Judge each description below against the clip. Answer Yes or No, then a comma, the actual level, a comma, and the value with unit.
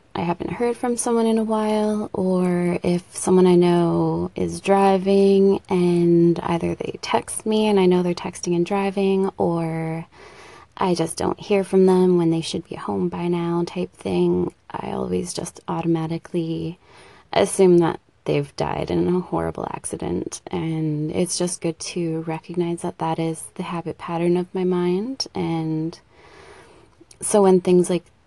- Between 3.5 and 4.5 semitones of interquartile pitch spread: No, average, 2.7 semitones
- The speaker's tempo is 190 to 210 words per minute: No, average, 160 wpm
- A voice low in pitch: No, medium, 175 Hz